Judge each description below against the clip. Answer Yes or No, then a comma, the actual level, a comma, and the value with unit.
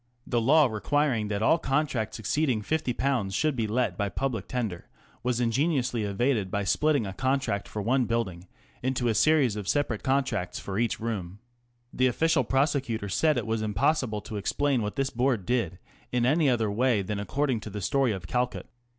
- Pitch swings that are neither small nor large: Yes, average, 4.6 semitones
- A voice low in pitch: Yes, low, 120 Hz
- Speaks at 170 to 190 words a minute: Yes, average, 185 wpm